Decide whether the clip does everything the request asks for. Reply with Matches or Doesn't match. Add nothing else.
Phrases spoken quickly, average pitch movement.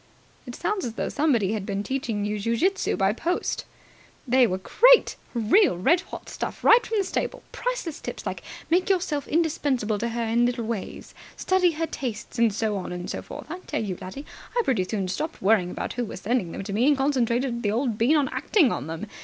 Doesn't match